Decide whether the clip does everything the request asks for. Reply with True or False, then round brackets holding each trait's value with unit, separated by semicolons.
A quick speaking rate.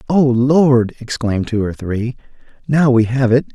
False (170 wpm)